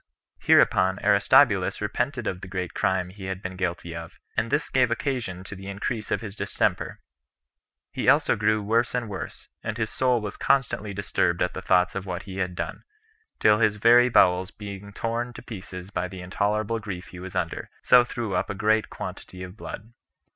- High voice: No, low, 100 Hz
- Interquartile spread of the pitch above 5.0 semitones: No, average, 3.6 semitones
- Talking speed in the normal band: Yes, average, 190 wpm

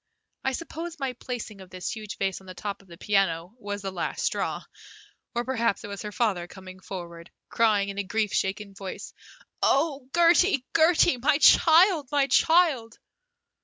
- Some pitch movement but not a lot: No, wide, 6.2 semitones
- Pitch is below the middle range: No, high, 215 Hz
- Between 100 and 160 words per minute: No, average, 170 wpm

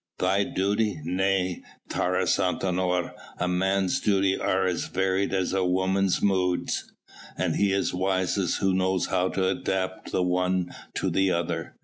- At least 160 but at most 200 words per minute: No, average, 145 wpm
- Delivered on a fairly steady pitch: Yes, narrow, 1.0 semitones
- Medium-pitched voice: No, very low, 95 Hz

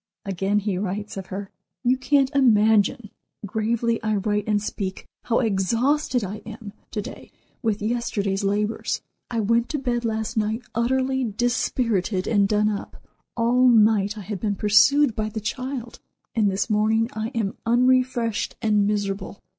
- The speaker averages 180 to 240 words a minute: No, average, 155 wpm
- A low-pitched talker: No, high, 220 Hz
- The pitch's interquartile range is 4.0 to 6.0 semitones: No, average, 2.7 semitones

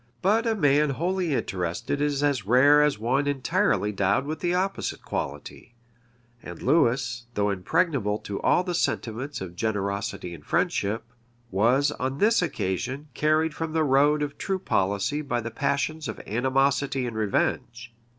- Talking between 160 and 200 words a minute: No, average, 150 wpm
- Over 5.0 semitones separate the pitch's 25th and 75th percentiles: Yes, wide, 5.4 semitones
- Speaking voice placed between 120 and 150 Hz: Yes, low, 135 Hz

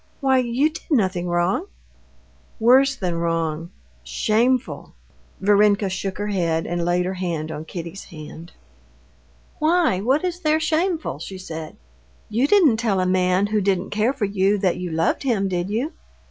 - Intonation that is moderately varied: No, wide, 6.4 semitones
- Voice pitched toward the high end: Yes, high, 195 Hz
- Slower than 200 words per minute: Yes, average, 155 wpm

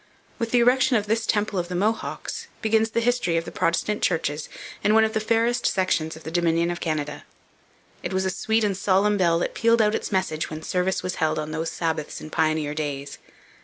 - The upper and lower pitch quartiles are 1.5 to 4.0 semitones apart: No, wide, 5.4 semitones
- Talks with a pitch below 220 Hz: Yes, medium, 185 Hz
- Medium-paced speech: No, fast, 215 wpm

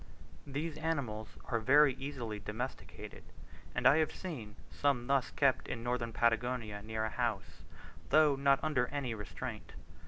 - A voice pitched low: Yes, low, 125 Hz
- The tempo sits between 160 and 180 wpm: No, average, 145 wpm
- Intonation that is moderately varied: Yes, average, 4.1 semitones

